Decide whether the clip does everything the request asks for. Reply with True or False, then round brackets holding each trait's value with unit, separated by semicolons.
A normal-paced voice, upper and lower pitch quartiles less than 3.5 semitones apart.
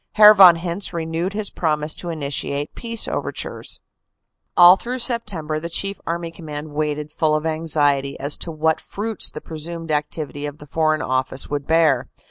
True (165 wpm; 2.7 semitones)